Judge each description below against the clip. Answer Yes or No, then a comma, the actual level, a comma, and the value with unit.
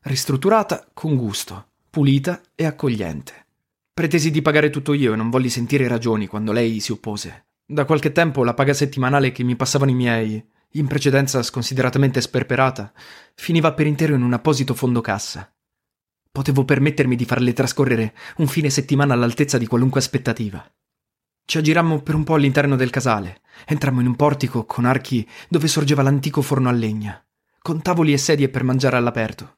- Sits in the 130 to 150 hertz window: Yes, low, 135 Hz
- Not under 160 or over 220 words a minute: Yes, average, 165 wpm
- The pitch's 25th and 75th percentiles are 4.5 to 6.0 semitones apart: No, average, 3.4 semitones